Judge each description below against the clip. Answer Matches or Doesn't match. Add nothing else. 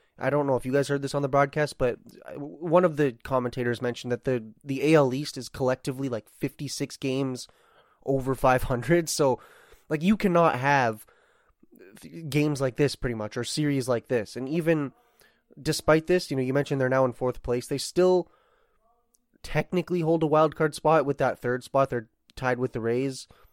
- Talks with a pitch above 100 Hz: Matches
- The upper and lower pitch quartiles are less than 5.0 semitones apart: Matches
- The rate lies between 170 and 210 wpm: Matches